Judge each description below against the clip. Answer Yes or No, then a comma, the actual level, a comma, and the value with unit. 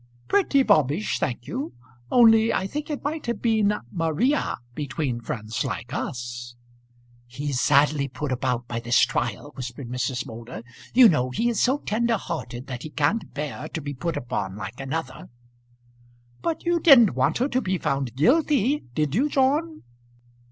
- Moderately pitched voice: Yes, medium, 150 Hz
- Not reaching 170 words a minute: Yes, average, 160 wpm